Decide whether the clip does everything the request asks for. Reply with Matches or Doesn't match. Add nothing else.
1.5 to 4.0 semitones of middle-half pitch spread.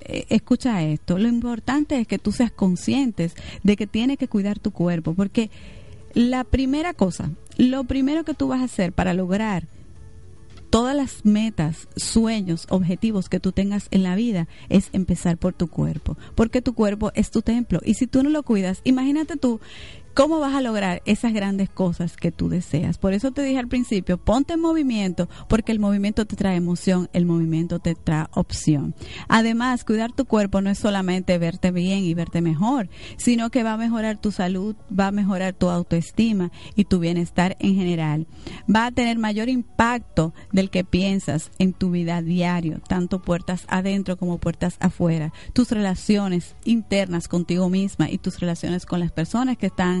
Doesn't match